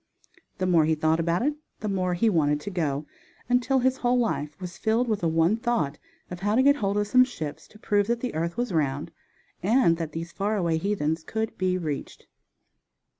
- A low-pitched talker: No, medium, 185 Hz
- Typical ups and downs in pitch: No, wide, 5.7 semitones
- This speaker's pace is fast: Yes, fast, 210 wpm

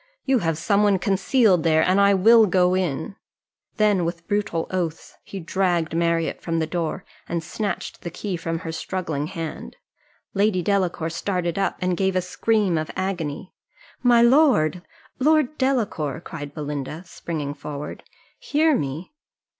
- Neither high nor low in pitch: Yes, medium, 180 Hz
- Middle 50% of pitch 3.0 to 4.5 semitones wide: Yes, average, 3.6 semitones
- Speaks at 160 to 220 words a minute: No, average, 150 wpm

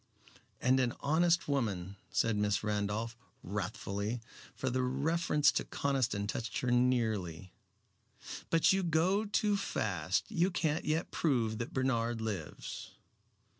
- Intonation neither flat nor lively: No, wide, 6.6 semitones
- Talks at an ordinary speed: No, slow, 125 wpm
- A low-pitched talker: Yes, low, 120 Hz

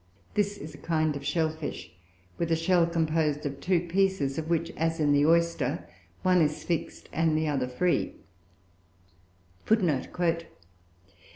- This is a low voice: No, medium, 160 Hz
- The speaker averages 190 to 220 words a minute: No, average, 145 wpm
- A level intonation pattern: Yes, narrow, 2.2 semitones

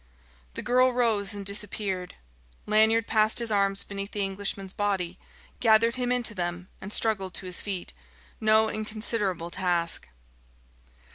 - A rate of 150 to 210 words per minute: No, slow, 135 wpm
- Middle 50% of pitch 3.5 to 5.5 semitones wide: No, narrow, 2.5 semitones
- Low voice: No, high, 205 Hz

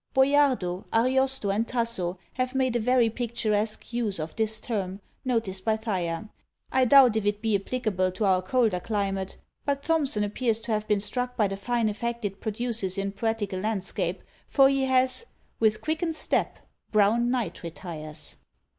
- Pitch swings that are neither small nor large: Yes, average, 4.1 semitones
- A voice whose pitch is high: Yes, high, 220 Hz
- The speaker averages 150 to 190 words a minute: Yes, average, 165 wpm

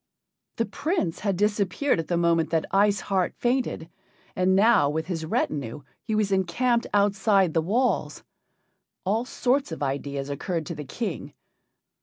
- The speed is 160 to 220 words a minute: No, average, 150 wpm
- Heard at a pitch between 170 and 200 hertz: Yes, high, 190 Hz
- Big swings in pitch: No, average, 5.0 semitones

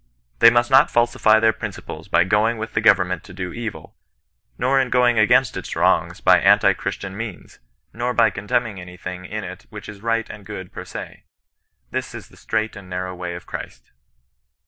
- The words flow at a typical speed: Yes, average, 190 wpm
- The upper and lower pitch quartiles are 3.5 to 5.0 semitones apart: Yes, average, 3.9 semitones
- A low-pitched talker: Yes, low, 105 Hz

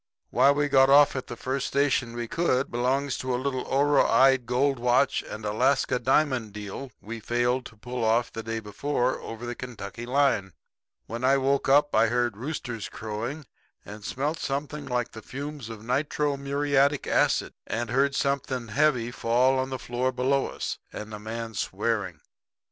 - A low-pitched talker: Yes, low, 130 Hz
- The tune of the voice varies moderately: Yes, average, 3.0 semitones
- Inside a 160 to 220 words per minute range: Yes, average, 170 wpm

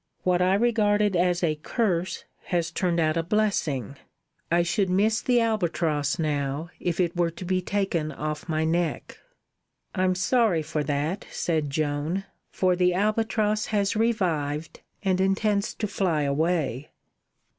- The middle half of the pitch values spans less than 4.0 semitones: No, average, 4.3 semitones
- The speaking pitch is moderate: Yes, medium, 175 Hz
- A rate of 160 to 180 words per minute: No, average, 145 wpm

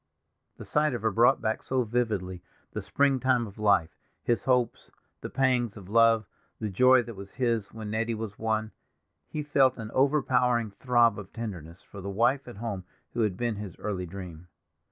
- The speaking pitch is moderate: No, low, 115 Hz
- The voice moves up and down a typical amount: Yes, average, 3.5 semitones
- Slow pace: No, average, 180 wpm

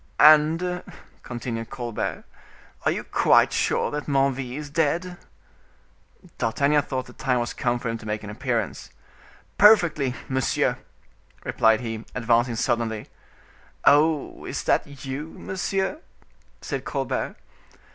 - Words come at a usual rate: No, slow, 115 wpm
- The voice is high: No, low, 130 Hz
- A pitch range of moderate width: Yes, average, 4.3 semitones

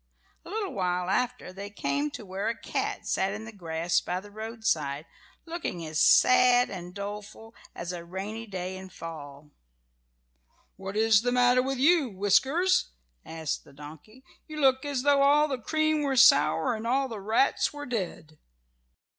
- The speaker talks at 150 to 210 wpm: Yes, average, 165 wpm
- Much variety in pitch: Yes, wide, 6.4 semitones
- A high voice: Yes, high, 215 Hz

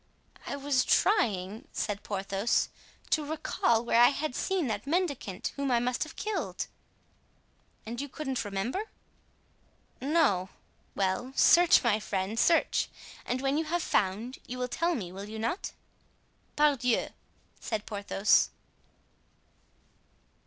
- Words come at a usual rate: No, slow, 125 wpm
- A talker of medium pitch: No, high, 245 Hz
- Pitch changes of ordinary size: No, wide, 6.1 semitones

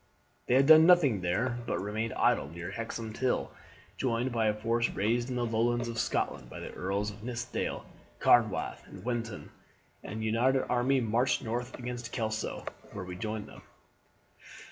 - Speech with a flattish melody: Yes, narrow, 2.2 semitones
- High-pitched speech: No, low, 115 Hz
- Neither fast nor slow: Yes, average, 165 wpm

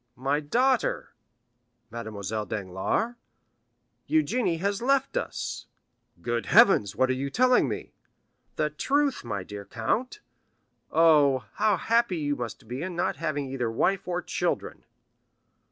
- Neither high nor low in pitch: Yes, medium, 150 Hz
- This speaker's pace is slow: Yes, slow, 125 wpm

